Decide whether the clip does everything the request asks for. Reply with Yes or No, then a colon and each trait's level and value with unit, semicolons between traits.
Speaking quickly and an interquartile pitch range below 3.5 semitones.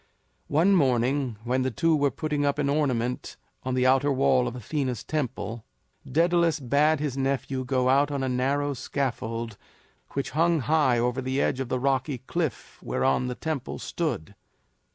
No: average, 165 wpm; average, 2.7 semitones